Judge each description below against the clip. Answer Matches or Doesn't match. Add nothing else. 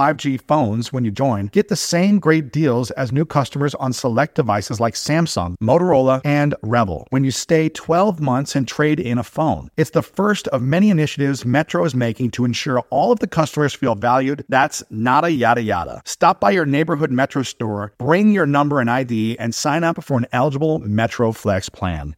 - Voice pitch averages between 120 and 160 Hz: Matches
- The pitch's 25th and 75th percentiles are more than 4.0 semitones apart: Matches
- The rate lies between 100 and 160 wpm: Doesn't match